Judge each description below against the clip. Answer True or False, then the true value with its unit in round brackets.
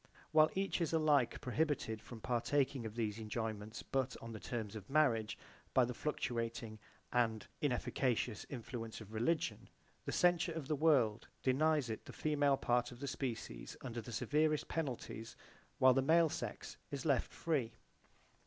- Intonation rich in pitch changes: False (4.8 semitones)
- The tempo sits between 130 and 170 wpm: True (160 wpm)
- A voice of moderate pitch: False (125 Hz)